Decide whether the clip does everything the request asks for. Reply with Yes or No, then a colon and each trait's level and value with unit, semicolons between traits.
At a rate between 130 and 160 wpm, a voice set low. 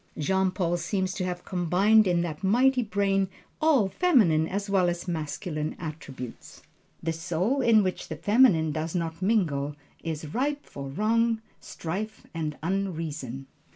No: average, 145 wpm; medium, 180 Hz